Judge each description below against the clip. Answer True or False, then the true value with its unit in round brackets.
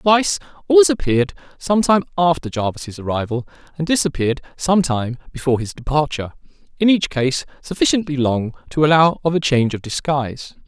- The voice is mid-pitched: True (150 Hz)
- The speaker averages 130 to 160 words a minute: True (150 wpm)